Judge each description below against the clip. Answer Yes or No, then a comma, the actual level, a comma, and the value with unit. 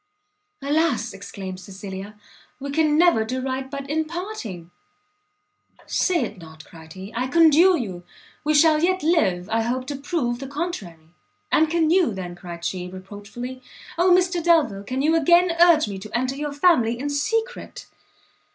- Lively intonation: Yes, wide, 8.4 semitones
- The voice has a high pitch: Yes, very high, 265 Hz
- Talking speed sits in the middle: Yes, average, 160 wpm